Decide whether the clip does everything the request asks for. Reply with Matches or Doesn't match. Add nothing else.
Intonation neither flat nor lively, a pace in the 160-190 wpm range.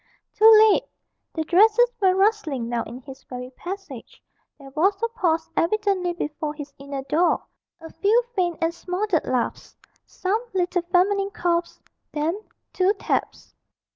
Doesn't match